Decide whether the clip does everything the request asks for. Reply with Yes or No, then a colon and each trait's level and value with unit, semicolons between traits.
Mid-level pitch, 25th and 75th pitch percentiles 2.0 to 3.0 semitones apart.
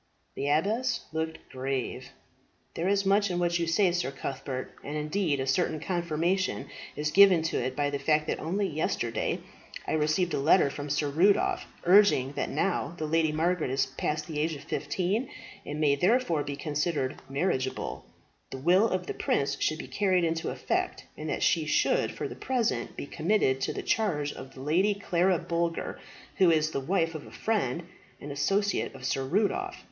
No: medium, 160 Hz; average, 4.7 semitones